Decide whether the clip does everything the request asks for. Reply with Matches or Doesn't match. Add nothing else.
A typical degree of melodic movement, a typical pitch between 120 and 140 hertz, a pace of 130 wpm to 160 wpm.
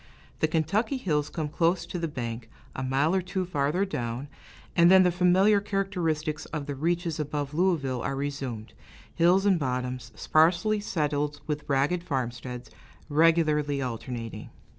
Doesn't match